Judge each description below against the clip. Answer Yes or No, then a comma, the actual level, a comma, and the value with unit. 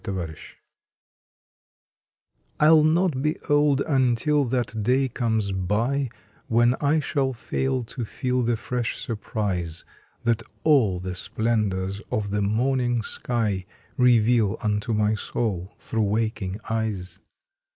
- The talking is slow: Yes, slow, 120 wpm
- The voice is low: Yes, low, 115 Hz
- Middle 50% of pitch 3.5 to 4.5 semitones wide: Yes, average, 4.0 semitones